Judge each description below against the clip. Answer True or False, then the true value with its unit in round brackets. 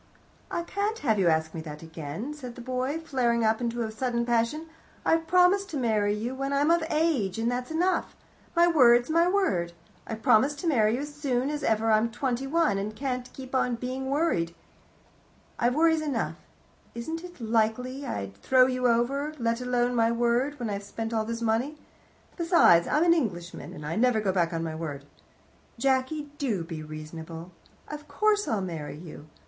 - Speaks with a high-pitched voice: True (245 Hz)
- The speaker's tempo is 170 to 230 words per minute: True (190 wpm)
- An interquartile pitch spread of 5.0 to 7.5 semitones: True (5.4 semitones)